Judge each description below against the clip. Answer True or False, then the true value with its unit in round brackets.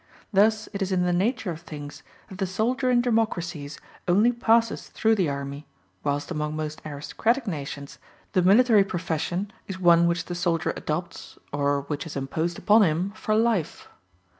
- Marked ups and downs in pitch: True (5.7 semitones)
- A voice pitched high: False (180 Hz)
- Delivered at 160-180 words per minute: True (165 wpm)